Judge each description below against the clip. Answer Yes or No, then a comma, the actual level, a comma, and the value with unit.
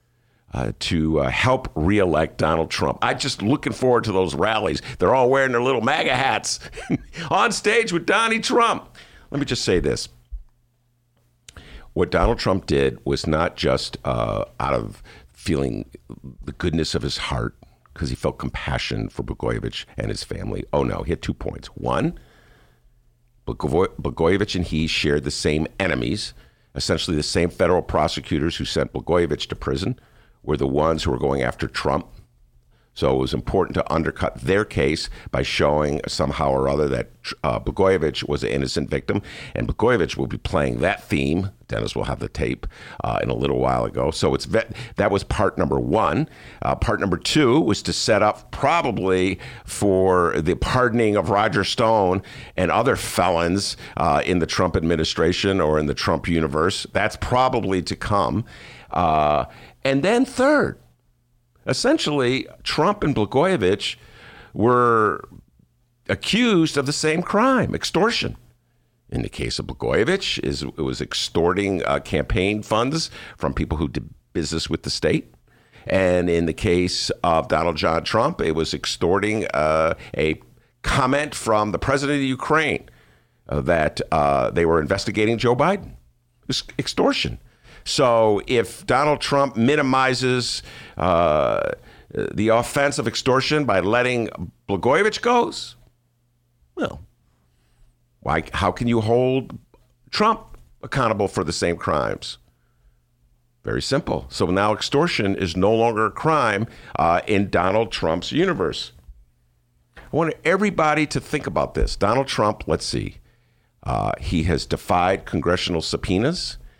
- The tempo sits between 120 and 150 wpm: Yes, average, 145 wpm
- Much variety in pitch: Yes, wide, 8.3 semitones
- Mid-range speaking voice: No, very low, 95 Hz